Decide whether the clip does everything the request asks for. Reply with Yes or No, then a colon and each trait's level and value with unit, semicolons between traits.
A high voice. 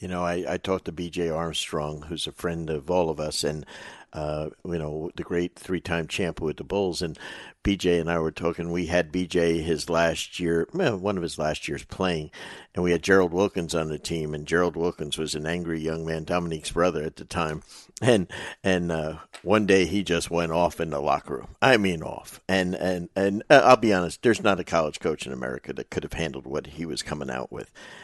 No: very low, 85 Hz